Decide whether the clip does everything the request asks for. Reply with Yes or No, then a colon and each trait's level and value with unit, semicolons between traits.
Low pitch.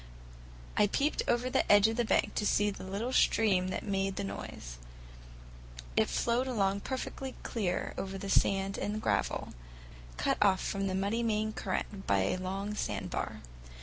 No: high, 200 Hz